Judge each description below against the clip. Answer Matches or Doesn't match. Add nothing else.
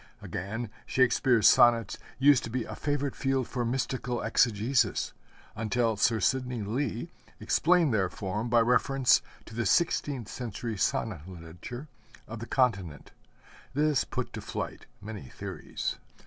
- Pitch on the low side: Matches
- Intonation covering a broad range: Doesn't match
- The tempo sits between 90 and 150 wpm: Matches